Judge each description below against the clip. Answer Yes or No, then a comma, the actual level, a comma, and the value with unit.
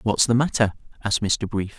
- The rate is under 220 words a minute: Yes, average, 200 wpm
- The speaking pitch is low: Yes, low, 110 Hz